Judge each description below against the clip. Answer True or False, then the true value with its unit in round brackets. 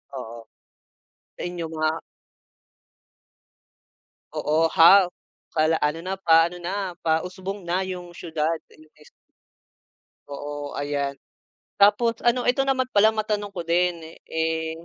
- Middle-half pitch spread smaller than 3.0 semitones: False (3.9 semitones)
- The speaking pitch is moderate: True (170 Hz)